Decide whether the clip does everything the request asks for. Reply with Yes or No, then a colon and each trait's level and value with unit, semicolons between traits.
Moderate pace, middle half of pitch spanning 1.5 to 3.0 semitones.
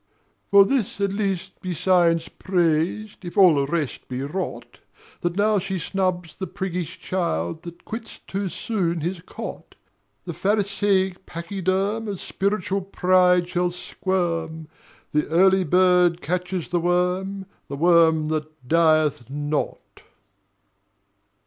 No: slow, 125 wpm; narrow, 2.6 semitones